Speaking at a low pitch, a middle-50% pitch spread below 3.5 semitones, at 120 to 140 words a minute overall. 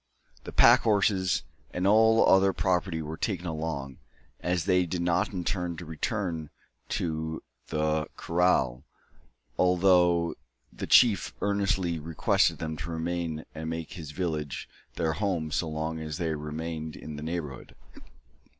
Yes: very low, 85 Hz; narrow, 2.6 semitones; slow, 135 wpm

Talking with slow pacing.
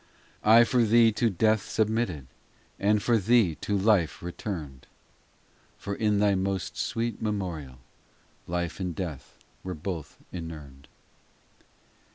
Yes: slow, 125 wpm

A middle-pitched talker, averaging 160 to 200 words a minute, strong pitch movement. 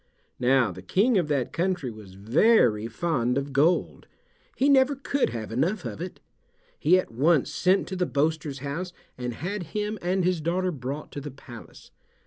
Yes: medium, 155 Hz; average, 175 wpm; wide, 6.6 semitones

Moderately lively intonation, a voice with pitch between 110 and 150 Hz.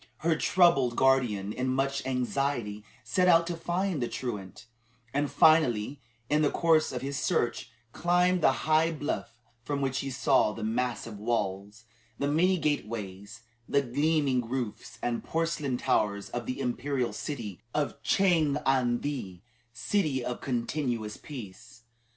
Yes: average, 4.6 semitones; low, 135 Hz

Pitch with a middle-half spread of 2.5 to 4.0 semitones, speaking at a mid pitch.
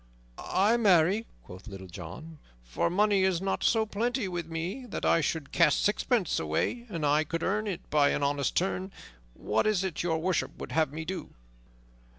No: average, 5.1 semitones; medium, 170 Hz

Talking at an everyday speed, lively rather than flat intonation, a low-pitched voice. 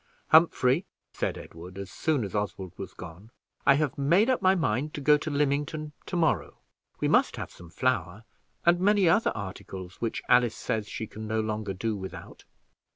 Yes: average, 180 wpm; wide, 7.6 semitones; low, 115 Hz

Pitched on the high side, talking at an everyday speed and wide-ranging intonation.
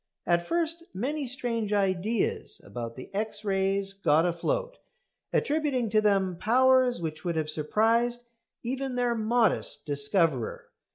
No: high, 215 Hz; slow, 125 wpm; wide, 6.0 semitones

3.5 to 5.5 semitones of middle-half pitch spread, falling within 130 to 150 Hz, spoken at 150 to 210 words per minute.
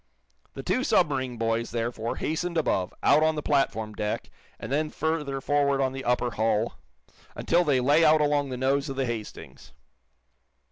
Yes: average, 4.3 semitones; low, 135 Hz; average, 170 wpm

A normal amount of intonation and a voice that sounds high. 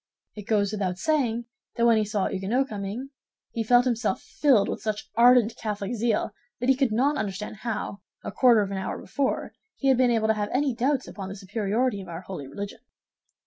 Yes: average, 3.6 semitones; high, 220 Hz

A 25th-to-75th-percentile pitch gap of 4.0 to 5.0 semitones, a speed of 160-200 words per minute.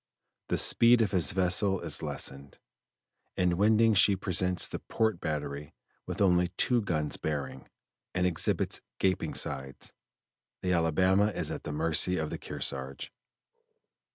No: average, 4.4 semitones; slow, 135 wpm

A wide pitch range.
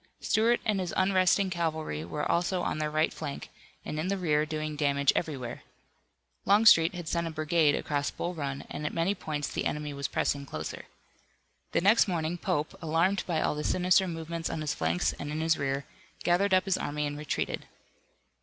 No: average, 3.3 semitones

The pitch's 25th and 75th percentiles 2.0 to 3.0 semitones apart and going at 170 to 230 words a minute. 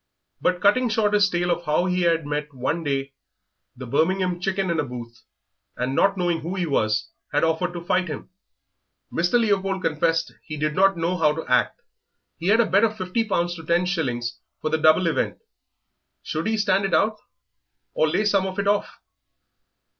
No: average, 4.0 semitones; average, 190 wpm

